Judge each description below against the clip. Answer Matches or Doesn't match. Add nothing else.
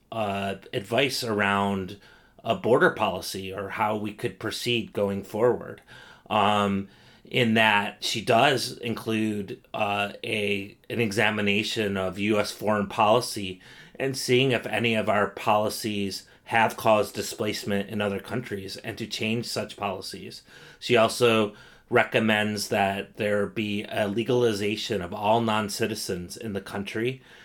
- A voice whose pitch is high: Doesn't match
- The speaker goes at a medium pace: Doesn't match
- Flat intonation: Matches